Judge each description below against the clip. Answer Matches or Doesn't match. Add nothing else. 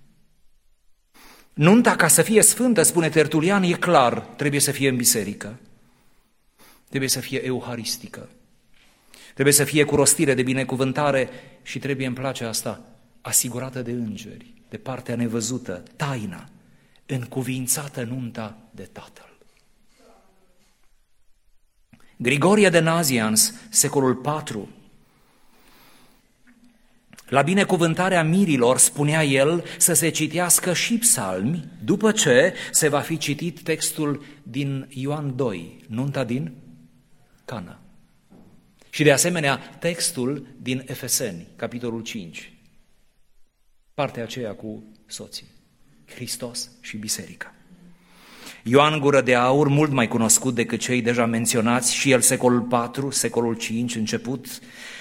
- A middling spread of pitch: Matches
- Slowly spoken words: Matches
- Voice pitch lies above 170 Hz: Doesn't match